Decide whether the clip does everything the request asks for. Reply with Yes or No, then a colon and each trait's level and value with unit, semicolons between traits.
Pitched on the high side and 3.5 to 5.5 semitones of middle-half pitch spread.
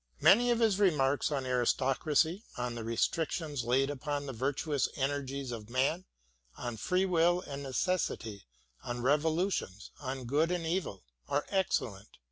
No: medium, 140 Hz; average, 4.8 semitones